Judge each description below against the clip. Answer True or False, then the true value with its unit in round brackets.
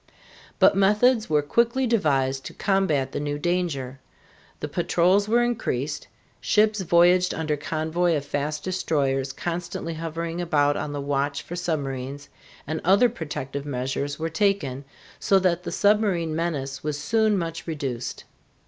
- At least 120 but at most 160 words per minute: True (140 wpm)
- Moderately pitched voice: True (160 Hz)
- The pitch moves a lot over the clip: False (4.5 semitones)